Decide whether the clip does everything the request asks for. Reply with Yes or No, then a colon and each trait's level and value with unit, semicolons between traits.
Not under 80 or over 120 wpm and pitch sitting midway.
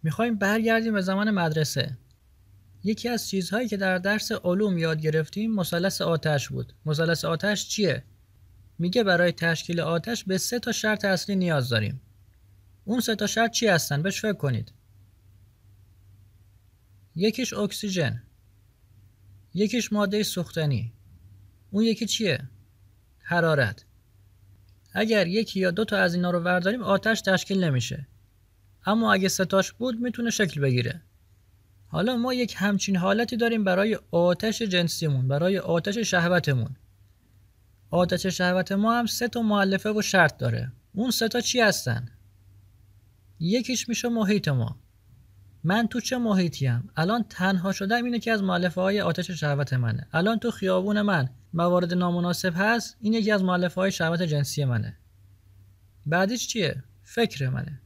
No: average, 140 wpm; medium, 175 Hz